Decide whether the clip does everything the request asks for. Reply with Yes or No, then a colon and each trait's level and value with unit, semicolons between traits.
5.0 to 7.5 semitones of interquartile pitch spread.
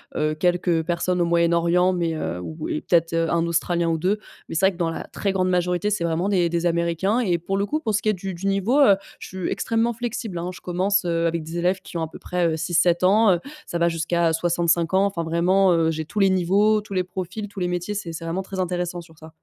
No: narrow, 2.4 semitones